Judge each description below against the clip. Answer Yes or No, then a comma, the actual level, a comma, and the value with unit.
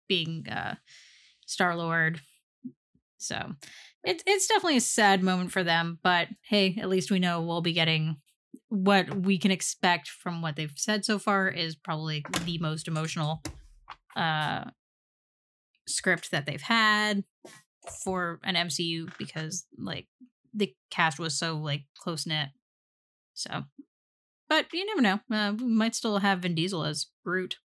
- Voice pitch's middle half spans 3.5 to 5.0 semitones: Yes, average, 4.0 semitones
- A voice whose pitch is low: No, medium, 180 Hz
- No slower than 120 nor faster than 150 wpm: Yes, average, 145 wpm